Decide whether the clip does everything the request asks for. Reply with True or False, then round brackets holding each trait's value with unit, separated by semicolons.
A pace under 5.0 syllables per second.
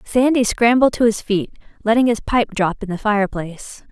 False (5.4 syllables/s)